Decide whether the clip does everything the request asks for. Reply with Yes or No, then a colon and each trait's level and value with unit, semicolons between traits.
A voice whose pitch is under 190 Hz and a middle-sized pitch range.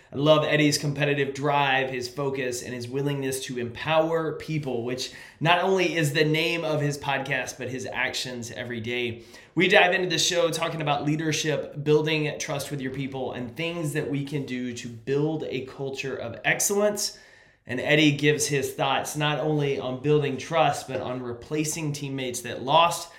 Yes: medium, 140 Hz; average, 3.3 semitones